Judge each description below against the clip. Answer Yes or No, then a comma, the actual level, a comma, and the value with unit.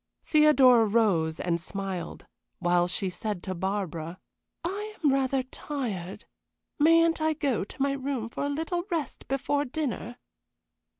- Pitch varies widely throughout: Yes, wide, 7.6 semitones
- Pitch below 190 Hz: No, very high, 255 Hz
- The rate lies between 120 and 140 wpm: Yes, slow, 135 wpm